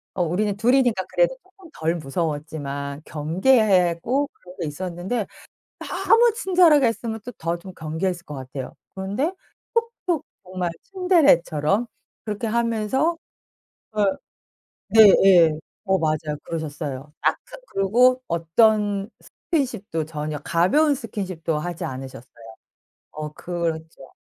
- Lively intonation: Yes, wide, 7.4 semitones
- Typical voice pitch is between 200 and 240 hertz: No, medium, 185 Hz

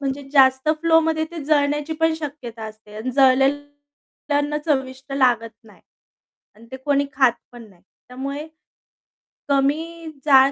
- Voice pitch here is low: No, very high, 275 Hz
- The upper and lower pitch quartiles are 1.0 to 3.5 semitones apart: Yes, narrow, 2.5 semitones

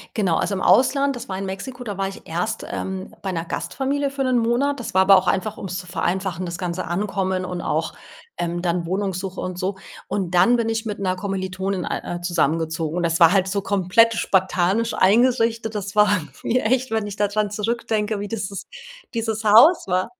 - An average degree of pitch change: Yes, average, 3.5 semitones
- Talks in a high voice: Yes, high, 195 Hz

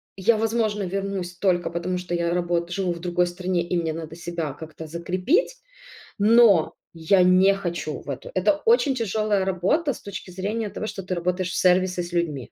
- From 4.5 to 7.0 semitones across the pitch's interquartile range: No, average, 2.7 semitones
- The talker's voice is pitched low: No, medium, 180 Hz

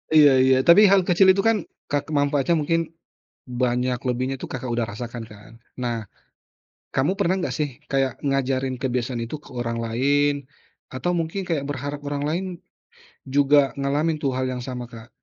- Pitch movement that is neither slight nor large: Yes, average, 3.2 semitones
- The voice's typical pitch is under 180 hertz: Yes, low, 135 Hz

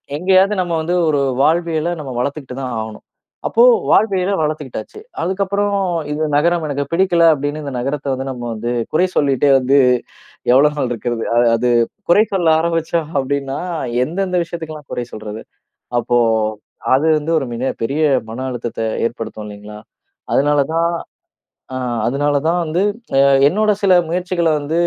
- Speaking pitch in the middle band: Yes, medium, 150 Hz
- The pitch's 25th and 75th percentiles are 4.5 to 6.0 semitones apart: Yes, average, 4.8 semitones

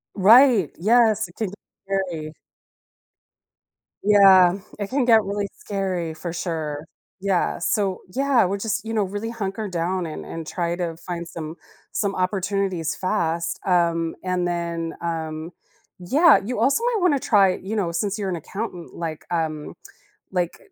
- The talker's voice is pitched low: No, medium, 185 Hz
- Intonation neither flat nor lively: Yes, average, 3.7 semitones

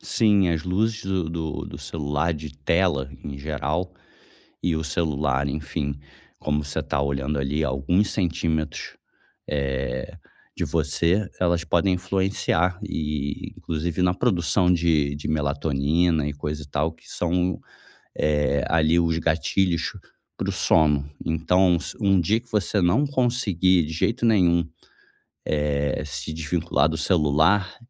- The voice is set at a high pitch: No, very low, 80 Hz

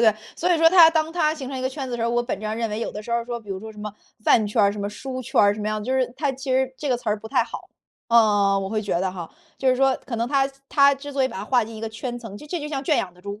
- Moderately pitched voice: No, high, 240 Hz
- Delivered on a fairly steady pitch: No, average, 4.2 semitones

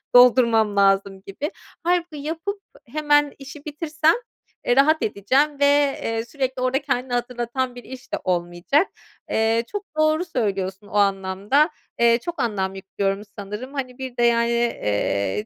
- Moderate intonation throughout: No, wide, 6.3 semitones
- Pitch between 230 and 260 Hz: Yes, high, 245 Hz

